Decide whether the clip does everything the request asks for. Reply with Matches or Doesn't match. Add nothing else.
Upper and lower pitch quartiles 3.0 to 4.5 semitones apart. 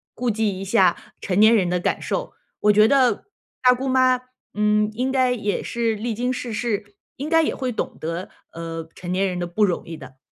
Doesn't match